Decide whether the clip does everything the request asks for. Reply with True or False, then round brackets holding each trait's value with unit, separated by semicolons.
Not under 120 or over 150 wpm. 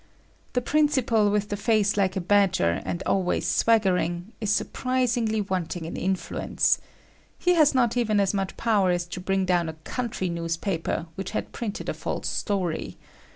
False (160 wpm)